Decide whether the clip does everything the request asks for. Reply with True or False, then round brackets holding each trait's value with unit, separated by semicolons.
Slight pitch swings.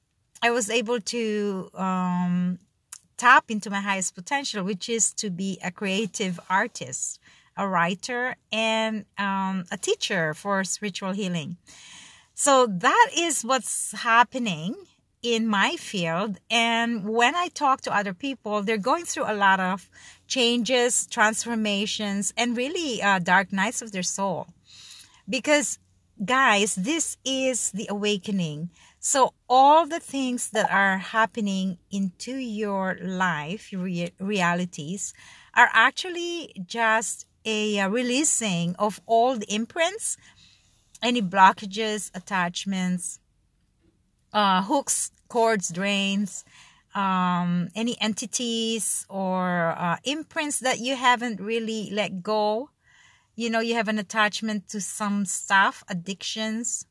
False (4.0 semitones)